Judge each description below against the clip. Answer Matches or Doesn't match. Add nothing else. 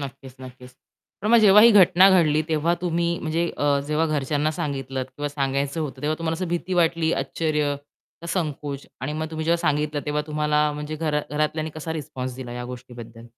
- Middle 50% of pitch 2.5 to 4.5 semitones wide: Matches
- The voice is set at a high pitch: Doesn't match